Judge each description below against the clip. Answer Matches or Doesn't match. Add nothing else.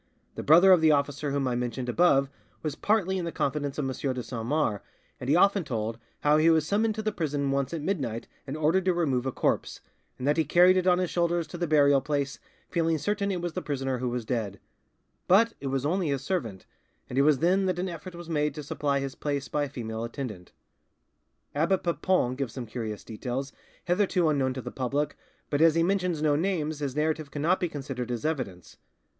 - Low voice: Doesn't match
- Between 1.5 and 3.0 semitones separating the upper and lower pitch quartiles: Doesn't match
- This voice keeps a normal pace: Doesn't match